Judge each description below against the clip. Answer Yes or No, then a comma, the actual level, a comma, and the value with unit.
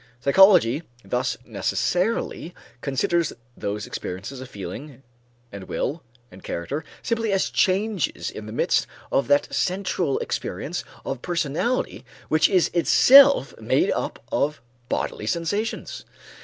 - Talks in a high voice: No, medium, 150 Hz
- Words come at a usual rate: No, slow, 115 wpm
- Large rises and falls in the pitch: Yes, wide, 7.3 semitones